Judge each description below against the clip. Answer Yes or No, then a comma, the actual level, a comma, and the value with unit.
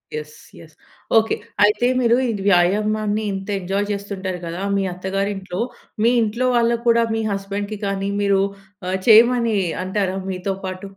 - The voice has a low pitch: No, high, 200 Hz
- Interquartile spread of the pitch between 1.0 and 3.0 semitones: Yes, narrow, 2.4 semitones